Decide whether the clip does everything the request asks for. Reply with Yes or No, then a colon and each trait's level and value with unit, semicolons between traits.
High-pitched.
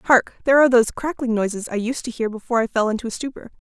Yes: high, 235 Hz